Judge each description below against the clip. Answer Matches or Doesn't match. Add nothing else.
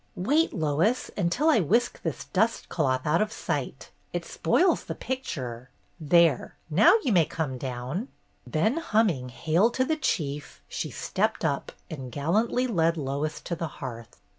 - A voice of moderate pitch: Matches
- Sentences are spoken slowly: Doesn't match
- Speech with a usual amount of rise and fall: Doesn't match